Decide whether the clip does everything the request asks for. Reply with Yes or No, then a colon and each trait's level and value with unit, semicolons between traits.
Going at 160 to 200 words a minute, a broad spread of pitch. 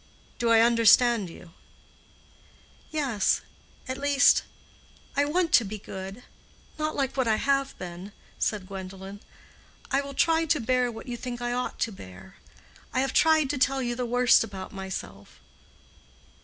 No: average, 145 wpm; wide, 5.7 semitones